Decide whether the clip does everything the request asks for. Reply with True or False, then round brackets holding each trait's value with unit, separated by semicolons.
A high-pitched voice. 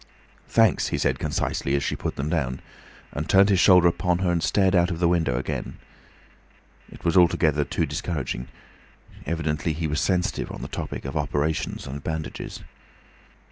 False (80 Hz)